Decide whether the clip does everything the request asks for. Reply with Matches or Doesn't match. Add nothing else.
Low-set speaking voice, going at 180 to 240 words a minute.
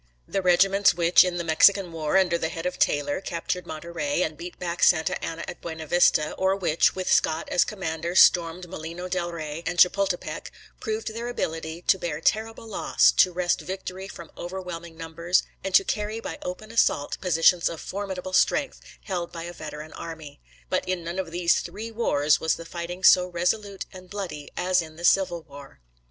Doesn't match